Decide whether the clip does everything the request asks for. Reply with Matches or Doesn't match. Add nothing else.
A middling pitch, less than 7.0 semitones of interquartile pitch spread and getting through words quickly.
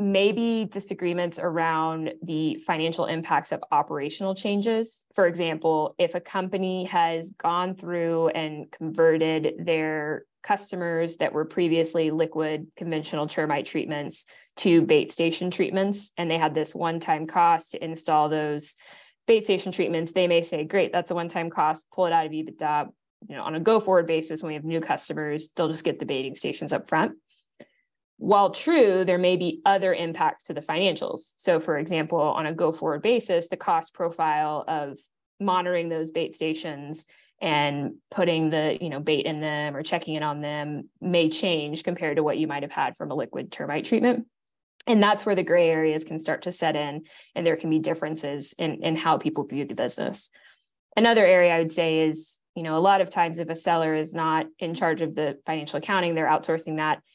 Doesn't match